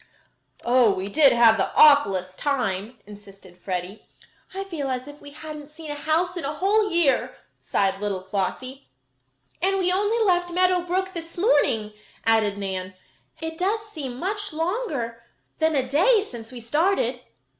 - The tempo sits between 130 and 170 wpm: Yes, average, 155 wpm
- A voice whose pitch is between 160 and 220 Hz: No, very high, 290 Hz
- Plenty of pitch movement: Yes, wide, 8.4 semitones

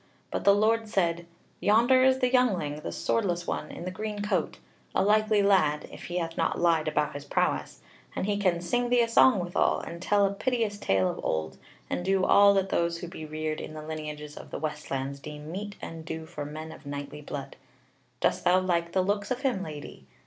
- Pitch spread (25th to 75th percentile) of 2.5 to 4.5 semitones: No, average, 4.9 semitones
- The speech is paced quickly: Yes, fast, 215 wpm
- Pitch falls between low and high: Yes, medium, 175 Hz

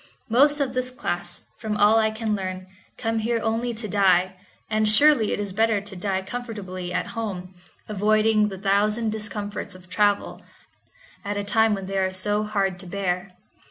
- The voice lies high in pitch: Yes, high, 210 Hz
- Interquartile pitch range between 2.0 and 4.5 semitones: Yes, narrow, 2.6 semitones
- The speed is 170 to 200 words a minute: Yes, average, 175 wpm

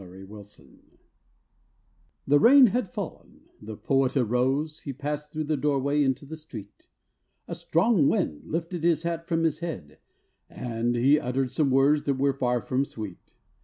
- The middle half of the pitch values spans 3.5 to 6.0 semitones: Yes, average, 4.3 semitones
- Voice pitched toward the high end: No, medium, 140 Hz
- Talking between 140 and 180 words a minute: Yes, average, 165 wpm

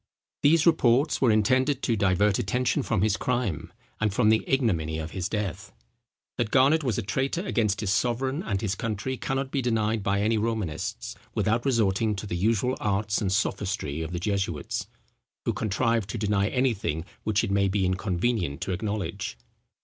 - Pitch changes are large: No, average, 3.8 semitones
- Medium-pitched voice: No, low, 105 Hz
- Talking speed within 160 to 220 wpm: Yes, average, 170 wpm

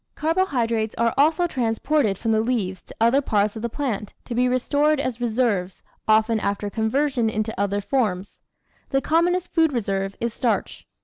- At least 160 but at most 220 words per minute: Yes, average, 170 wpm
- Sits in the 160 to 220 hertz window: No, high, 230 Hz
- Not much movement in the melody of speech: No, average, 4.3 semitones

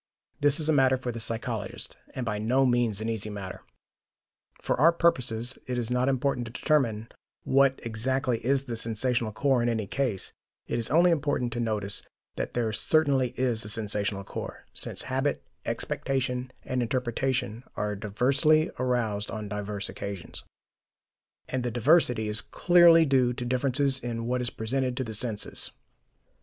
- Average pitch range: Yes, average, 3.2 semitones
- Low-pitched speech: Yes, low, 125 Hz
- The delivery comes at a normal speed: Yes, average, 160 wpm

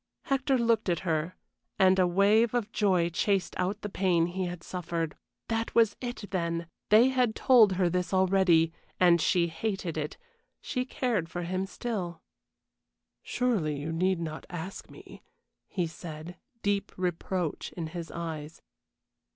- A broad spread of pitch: No, average, 3.7 semitones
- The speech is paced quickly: No, average, 150 wpm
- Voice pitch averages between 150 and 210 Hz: Yes, medium, 185 Hz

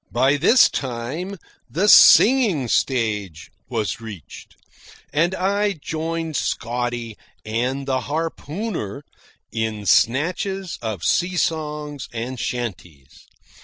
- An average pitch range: No, wide, 6.3 semitones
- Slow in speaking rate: Yes, slow, 95 wpm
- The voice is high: No, low, 135 Hz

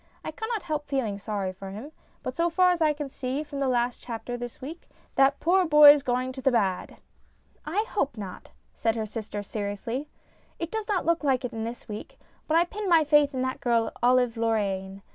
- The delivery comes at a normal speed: No, fast, 210 wpm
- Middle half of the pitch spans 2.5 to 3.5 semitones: No, average, 5.1 semitones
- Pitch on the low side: No, very high, 255 Hz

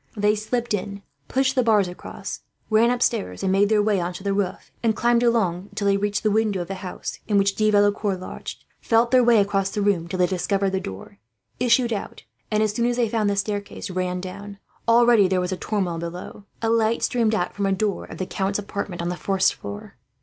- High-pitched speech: Yes, high, 205 Hz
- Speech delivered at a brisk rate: Yes, fast, 230 wpm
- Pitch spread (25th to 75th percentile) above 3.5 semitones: No, average, 2.7 semitones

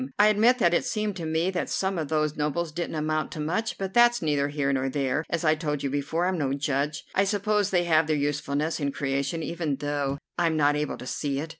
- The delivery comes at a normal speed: No, fast, 240 wpm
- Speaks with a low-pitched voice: No, medium, 155 Hz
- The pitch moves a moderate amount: Yes, average, 3.5 semitones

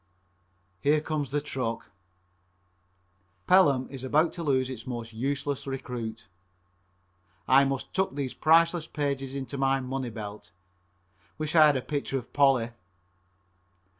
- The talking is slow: Yes, slow, 130 wpm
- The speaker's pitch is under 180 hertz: Yes, low, 135 Hz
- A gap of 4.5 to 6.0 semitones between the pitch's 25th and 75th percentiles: No, narrow, 2.5 semitones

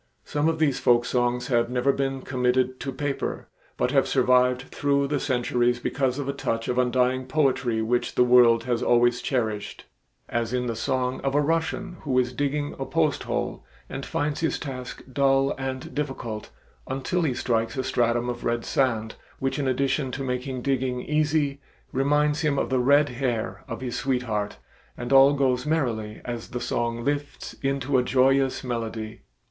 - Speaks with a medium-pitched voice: No, low, 130 Hz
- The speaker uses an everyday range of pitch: No, narrow, 2.2 semitones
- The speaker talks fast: No, average, 175 wpm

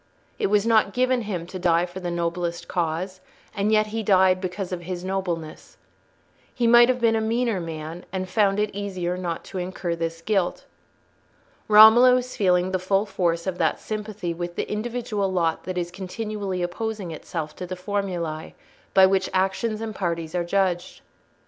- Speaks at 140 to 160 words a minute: No, average, 175 wpm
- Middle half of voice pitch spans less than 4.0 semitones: Yes, average, 3.3 semitones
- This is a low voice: No, medium, 185 Hz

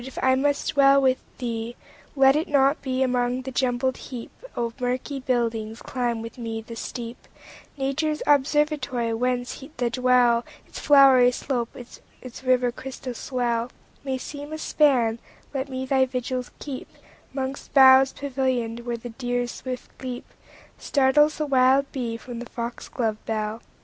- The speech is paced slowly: Yes, slow, 130 wpm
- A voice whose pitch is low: No, very high, 255 Hz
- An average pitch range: No, narrow, 2.1 semitones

